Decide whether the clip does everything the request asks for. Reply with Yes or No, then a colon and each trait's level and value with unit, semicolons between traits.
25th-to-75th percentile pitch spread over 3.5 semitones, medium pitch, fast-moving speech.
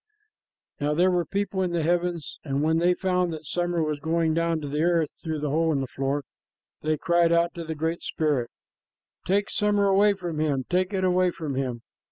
No: average, 2.9 semitones; medium, 165 Hz; fast, 210 wpm